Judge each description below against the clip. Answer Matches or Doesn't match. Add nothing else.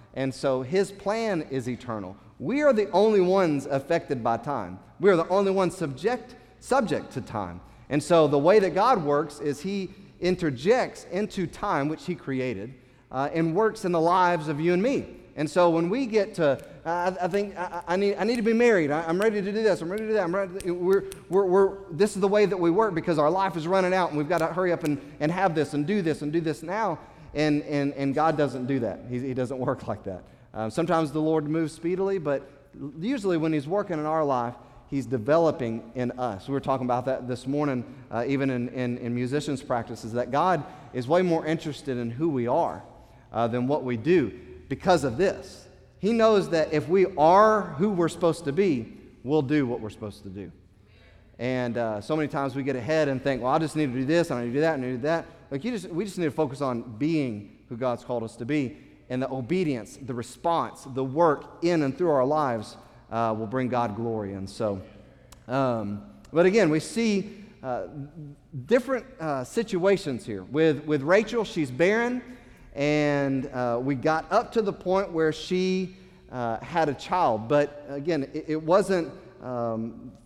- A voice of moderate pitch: Matches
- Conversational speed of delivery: Doesn't match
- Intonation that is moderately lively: Doesn't match